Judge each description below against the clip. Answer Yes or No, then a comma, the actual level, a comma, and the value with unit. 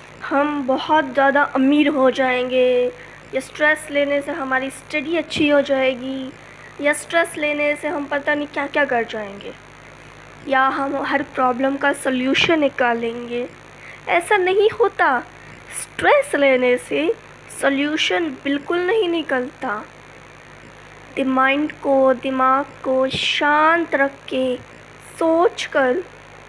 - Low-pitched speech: No, very high, 280 Hz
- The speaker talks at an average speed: Yes, average, 120 wpm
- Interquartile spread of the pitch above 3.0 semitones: No, narrow, 2.4 semitones